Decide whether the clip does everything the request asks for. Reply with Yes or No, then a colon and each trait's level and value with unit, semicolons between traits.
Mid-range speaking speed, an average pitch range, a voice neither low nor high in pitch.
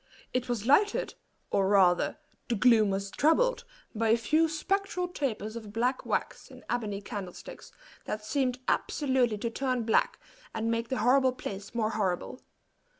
No: average, 150 wpm; average, 4.0 semitones; high, 235 Hz